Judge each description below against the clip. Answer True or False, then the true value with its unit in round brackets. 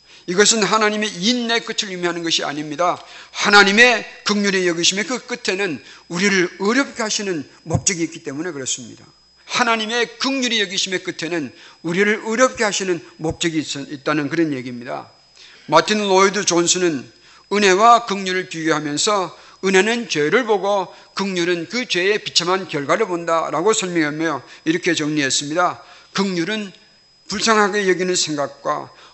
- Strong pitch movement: False (4.2 semitones)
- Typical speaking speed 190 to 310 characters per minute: False (335 characters per minute)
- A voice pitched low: False (190 Hz)